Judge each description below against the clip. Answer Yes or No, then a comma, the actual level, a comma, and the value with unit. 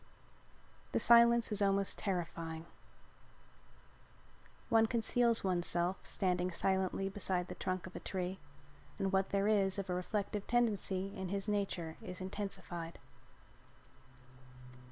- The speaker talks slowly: Yes, slow, 115 wpm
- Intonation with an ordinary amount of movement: No, narrow, 2.1 semitones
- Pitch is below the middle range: No, high, 195 Hz